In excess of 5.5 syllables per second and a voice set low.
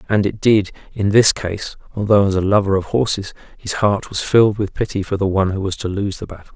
Yes: 5.8 syllables/s; low, 100 Hz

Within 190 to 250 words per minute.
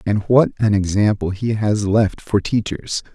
No: average, 170 wpm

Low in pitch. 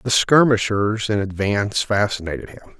Yes: low, 105 Hz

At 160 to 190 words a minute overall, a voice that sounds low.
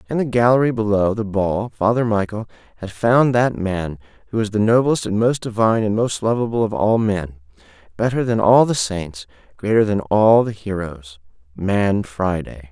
Yes: average, 170 wpm; low, 105 Hz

